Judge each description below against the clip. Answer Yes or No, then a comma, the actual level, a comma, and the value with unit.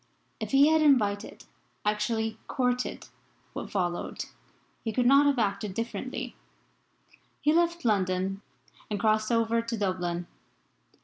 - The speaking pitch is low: No, high, 225 Hz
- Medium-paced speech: No, slow, 120 wpm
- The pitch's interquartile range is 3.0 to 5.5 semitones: Yes, average, 3.8 semitones